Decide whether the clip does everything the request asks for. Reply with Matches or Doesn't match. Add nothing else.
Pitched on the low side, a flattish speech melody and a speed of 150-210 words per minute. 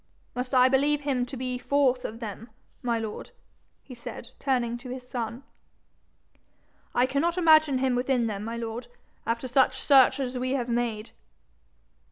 Doesn't match